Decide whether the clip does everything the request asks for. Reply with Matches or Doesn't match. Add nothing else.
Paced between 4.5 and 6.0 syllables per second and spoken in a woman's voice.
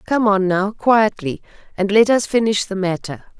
Matches